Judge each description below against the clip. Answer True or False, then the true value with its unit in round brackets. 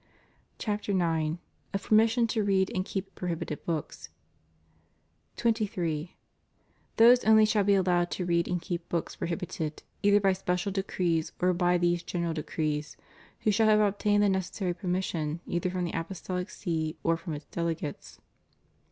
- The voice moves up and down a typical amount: True (3.2 semitones)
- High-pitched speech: False (180 Hz)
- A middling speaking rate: True (150 wpm)